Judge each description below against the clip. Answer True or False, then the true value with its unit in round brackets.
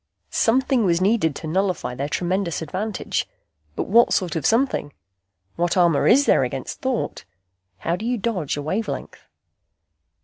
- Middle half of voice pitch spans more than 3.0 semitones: True (5.5 semitones)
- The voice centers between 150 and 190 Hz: True (185 Hz)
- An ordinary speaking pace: True (145 wpm)